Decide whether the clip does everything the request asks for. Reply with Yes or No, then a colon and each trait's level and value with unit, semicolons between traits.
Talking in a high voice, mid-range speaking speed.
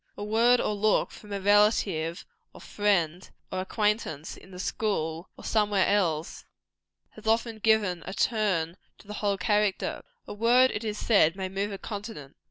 Yes: high, 205 Hz; average, 175 wpm